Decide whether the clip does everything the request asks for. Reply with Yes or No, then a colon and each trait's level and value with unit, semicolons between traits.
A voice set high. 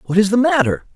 Yes: high, 195 Hz